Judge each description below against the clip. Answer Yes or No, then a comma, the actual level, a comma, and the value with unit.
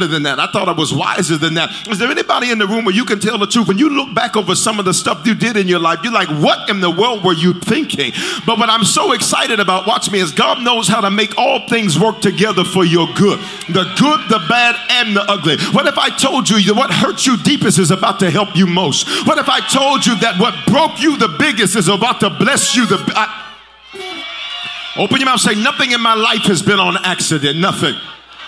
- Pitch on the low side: No, high, 215 Hz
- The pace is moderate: No, fast, 255 wpm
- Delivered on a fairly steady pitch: No, average, 4.1 semitones